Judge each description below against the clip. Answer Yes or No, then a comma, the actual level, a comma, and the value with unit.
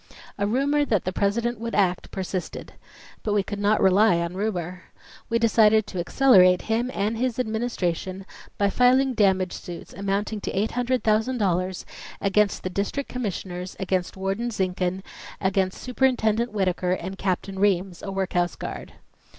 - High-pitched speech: Yes, high, 200 Hz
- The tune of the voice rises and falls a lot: No, average, 3.3 semitones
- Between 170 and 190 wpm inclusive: No, average, 140 wpm